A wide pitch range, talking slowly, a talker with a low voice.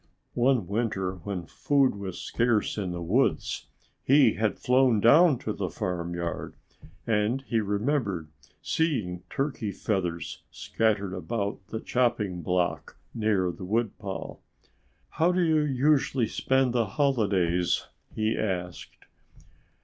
Yes: wide, 5.7 semitones; slow, 120 wpm; low, 110 Hz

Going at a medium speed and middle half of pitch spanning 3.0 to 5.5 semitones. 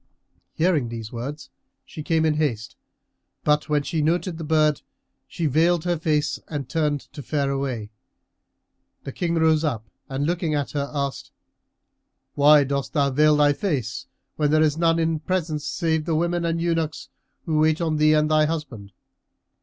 No: average, 170 wpm; narrow, 2.4 semitones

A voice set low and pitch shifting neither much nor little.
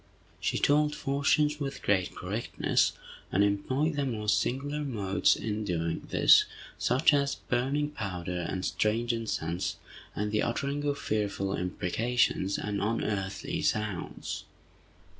No: low, 110 Hz; wide, 6.1 semitones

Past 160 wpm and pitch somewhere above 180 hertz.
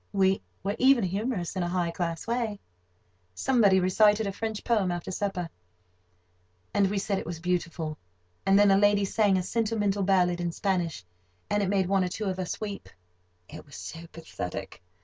Yes: average, 170 wpm; high, 190 Hz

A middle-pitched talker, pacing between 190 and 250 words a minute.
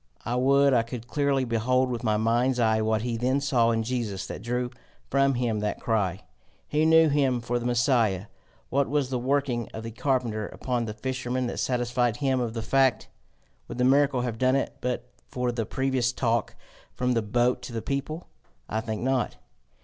No: low, 125 Hz; average, 195 wpm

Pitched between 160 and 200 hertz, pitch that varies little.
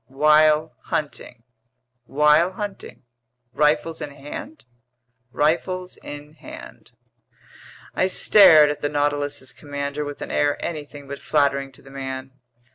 No: medium, 145 Hz; narrow, 1.5 semitones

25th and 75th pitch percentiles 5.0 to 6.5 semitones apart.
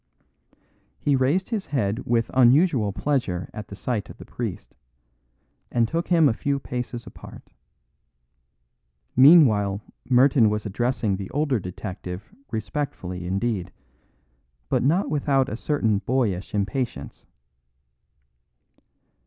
Yes: wide, 5.4 semitones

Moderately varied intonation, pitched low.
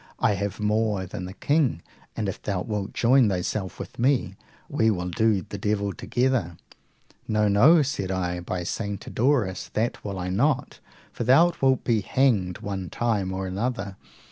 Yes: average, 4.2 semitones; low, 105 Hz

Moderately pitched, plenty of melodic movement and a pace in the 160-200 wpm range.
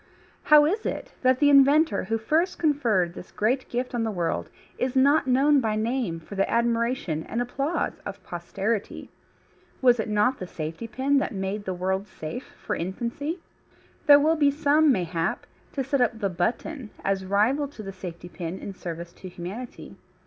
No: high, 230 Hz; wide, 6.5 semitones; average, 180 wpm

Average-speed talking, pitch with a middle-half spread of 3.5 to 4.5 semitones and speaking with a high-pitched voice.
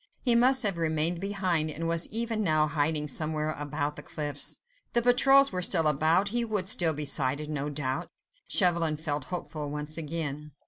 No: average, 175 wpm; average, 4.1 semitones; medium, 160 Hz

